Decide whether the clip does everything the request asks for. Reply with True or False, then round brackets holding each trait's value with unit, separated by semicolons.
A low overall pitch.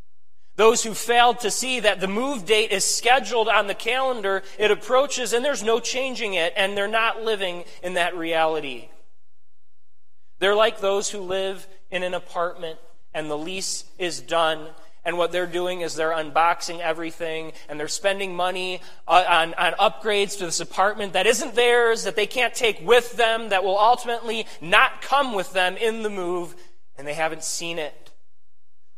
False (185 Hz)